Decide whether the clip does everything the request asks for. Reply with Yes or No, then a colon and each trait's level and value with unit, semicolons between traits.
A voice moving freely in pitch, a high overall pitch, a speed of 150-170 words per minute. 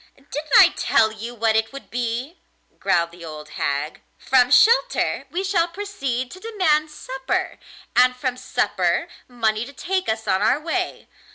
Yes: wide, 7.2 semitones; very high, 255 Hz; average, 160 wpm